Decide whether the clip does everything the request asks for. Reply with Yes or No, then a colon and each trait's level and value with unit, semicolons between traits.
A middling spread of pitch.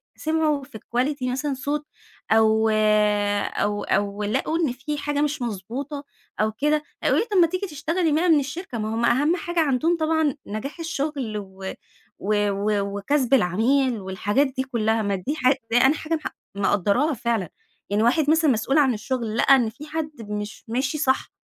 No: wide, 5.7 semitones